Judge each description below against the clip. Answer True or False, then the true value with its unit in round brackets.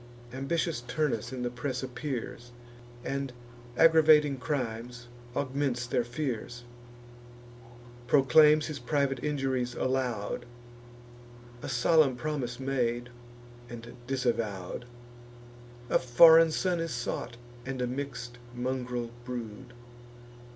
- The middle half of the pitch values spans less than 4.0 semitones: True (3.0 semitones)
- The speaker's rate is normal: False (95 wpm)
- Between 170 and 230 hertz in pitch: False (130 Hz)